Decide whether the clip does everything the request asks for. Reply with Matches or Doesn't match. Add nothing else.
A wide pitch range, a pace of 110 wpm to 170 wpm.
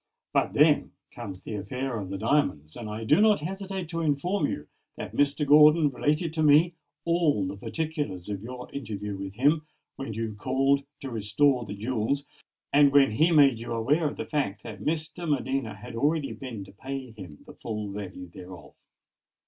Doesn't match